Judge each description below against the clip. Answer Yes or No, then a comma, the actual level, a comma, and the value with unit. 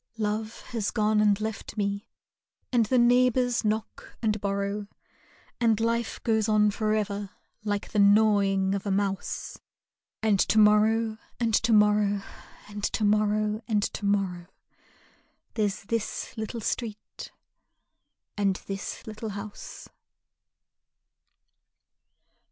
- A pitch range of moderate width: No, narrow, 1.5 semitones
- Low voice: No, high, 210 Hz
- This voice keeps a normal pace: No, slow, 115 wpm